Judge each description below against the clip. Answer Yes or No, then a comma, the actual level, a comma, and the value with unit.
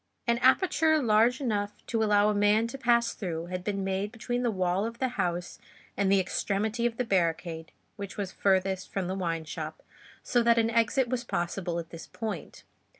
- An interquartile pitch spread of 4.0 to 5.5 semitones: Yes, average, 4.4 semitones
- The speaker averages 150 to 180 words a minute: No, average, 195 wpm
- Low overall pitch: No, high, 205 Hz